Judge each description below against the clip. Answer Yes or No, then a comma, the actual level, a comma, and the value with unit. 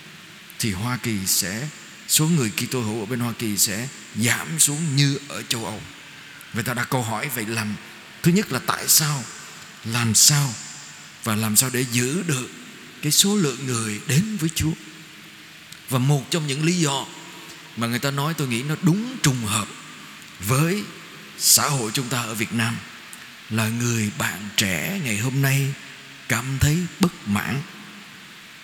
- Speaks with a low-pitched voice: Yes, low, 130 Hz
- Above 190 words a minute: No, average, 170 wpm